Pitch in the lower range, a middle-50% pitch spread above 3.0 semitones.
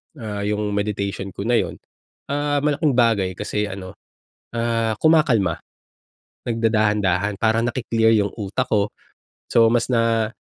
No: low, 110 Hz; narrow, 2.5 semitones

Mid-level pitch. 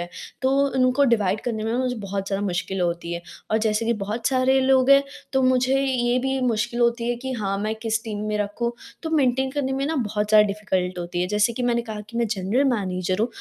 No: high, 230 Hz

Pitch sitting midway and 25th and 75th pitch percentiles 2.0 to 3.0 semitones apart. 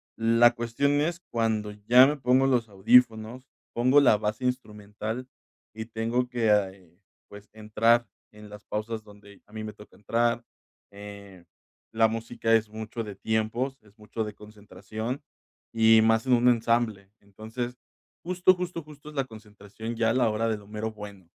No: low, 110 Hz; narrow, 2.4 semitones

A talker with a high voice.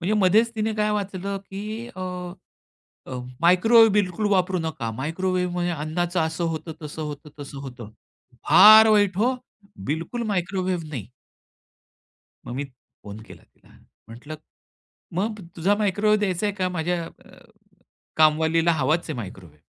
No: medium, 180 Hz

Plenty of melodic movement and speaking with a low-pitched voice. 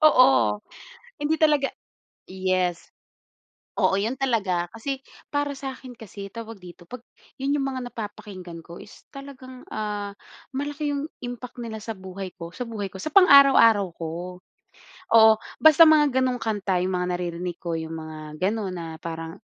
No: wide, 6.9 semitones; high, 215 Hz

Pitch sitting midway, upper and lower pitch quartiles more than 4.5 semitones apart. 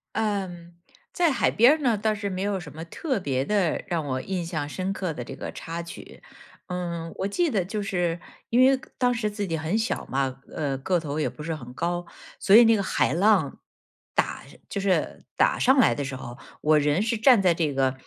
Yes: medium, 180 Hz; average, 5.2 semitones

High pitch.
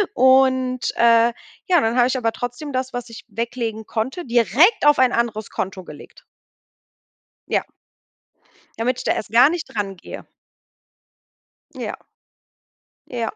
Yes: high, 240 Hz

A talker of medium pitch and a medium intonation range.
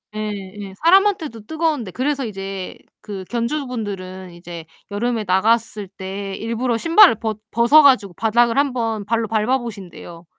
No: high, 225 Hz; average, 4.1 semitones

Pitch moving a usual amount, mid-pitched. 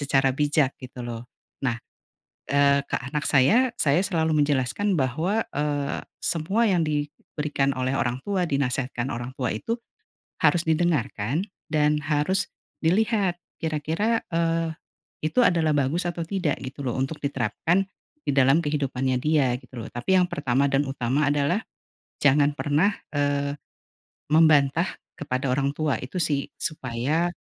Yes: average, 3.2 semitones; medium, 145 Hz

